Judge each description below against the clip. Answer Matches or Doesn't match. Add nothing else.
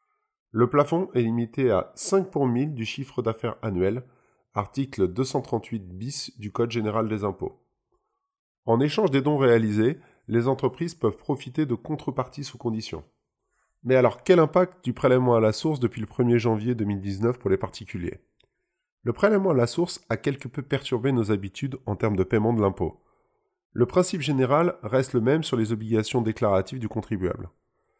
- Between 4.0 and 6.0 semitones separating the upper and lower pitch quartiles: Matches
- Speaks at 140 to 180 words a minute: Matches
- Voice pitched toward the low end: Matches